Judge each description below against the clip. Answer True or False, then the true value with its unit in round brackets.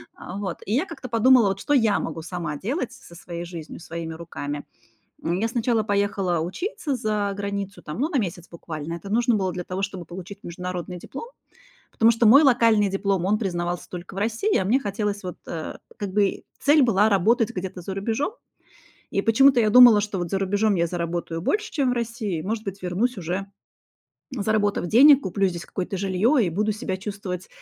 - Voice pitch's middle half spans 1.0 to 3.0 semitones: False (4.2 semitones)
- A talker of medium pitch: False (200 Hz)